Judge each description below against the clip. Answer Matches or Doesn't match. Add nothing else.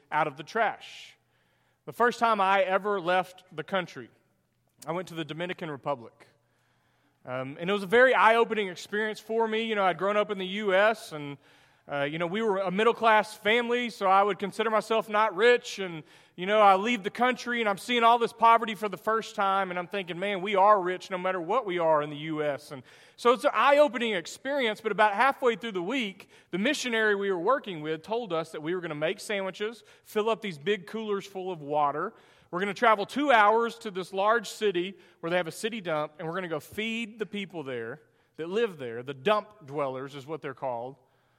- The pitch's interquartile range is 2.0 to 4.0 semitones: Doesn't match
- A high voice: Matches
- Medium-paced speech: Doesn't match